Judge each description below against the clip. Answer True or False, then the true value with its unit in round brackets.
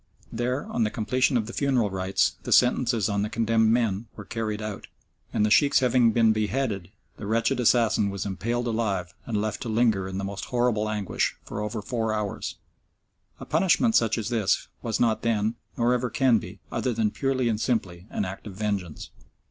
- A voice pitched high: False (110 Hz)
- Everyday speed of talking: True (195 wpm)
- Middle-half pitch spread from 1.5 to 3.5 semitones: True (2.7 semitones)